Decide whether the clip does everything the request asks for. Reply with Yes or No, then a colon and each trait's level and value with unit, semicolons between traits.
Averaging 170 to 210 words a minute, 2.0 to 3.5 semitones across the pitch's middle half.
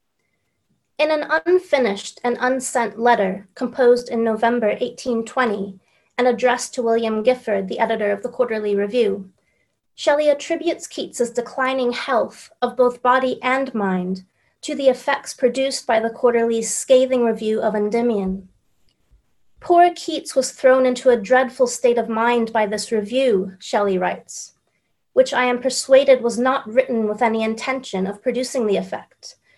No: average, 145 wpm; average, 2.8 semitones